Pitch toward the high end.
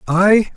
Yes: high, 195 Hz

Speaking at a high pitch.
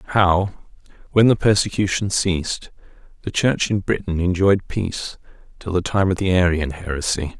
No: very low, 95 Hz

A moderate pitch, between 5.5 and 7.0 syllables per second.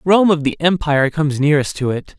Yes: medium, 155 Hz; 6.2 syllables/s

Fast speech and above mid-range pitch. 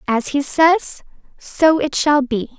No: average, 165 wpm; very high, 280 Hz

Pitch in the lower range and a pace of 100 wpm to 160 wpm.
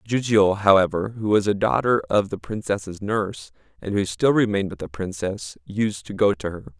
No: low, 100 Hz; average, 195 wpm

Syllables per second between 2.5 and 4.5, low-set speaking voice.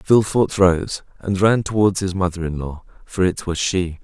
No: 4.8 syllables/s; very low, 95 Hz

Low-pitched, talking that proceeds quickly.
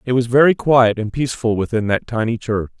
Yes: low, 115 Hz; fast, 215 wpm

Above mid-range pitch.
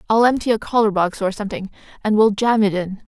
Yes: high, 210 Hz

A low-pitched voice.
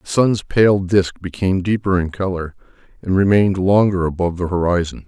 Yes: very low, 95 Hz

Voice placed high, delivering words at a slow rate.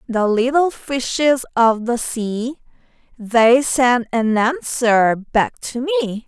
Yes: high, 245 Hz; slow, 125 wpm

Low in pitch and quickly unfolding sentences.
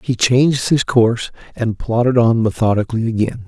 No: low, 115 Hz; average, 155 wpm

